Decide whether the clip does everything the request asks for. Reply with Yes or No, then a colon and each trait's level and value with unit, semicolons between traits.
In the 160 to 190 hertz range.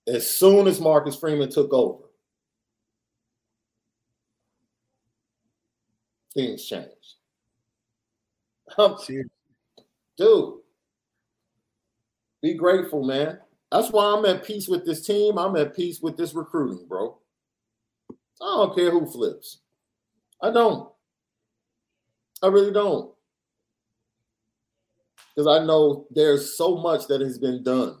No: medium, 140 Hz